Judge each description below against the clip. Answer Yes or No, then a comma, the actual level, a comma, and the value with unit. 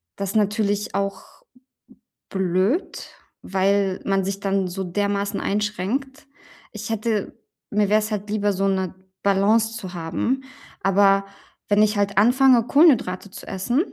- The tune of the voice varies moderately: No, narrow, 1.9 semitones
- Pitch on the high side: Yes, high, 200 Hz